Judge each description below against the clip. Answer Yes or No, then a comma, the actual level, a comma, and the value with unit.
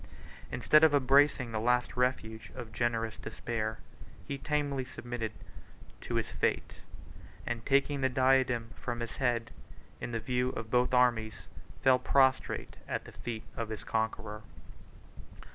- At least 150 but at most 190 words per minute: No, average, 140 wpm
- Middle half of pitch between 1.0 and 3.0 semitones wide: Yes, narrow, 2.6 semitones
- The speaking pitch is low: Yes, low, 120 Hz